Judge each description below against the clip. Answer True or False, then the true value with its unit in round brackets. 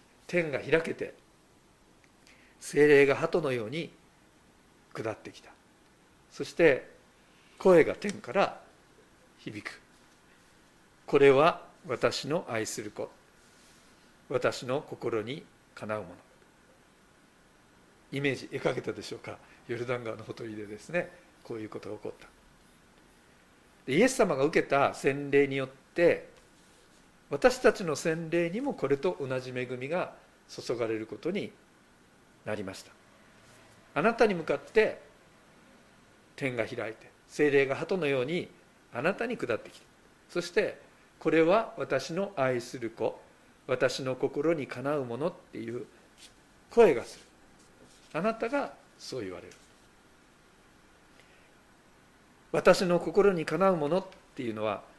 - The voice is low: False (145 Hz)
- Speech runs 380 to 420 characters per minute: False (230 characters per minute)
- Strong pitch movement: True (6.5 semitones)